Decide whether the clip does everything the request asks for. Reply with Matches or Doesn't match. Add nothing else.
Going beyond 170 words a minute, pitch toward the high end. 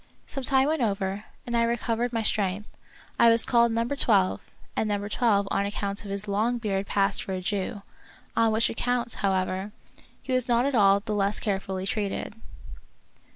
Matches